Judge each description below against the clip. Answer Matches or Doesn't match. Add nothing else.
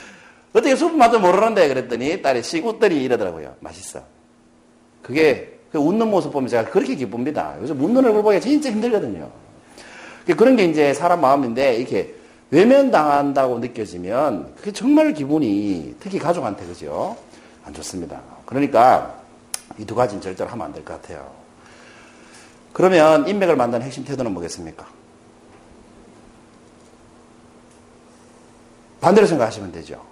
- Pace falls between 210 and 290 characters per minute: Doesn't match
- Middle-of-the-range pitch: Matches